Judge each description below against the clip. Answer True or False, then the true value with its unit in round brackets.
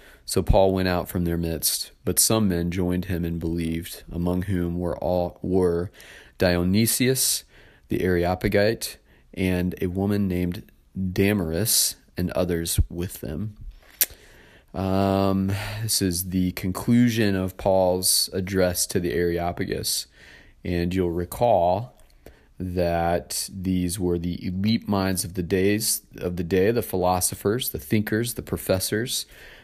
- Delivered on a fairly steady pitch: True (2.0 semitones)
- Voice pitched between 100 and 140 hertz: False (90 Hz)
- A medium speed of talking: False (130 wpm)